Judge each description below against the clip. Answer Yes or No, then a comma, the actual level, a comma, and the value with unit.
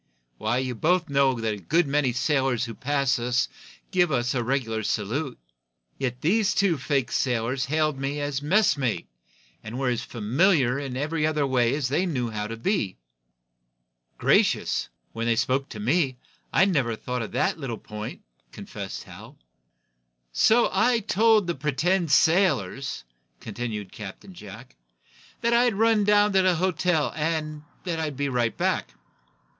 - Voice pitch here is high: No, medium, 140 Hz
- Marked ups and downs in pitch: Yes, wide, 6.0 semitones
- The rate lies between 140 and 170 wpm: Yes, average, 155 wpm